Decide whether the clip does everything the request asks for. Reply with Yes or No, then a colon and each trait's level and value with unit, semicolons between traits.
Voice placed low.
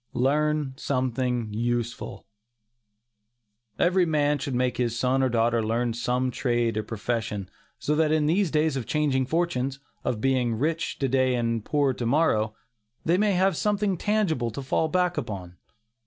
Yes: low, 130 Hz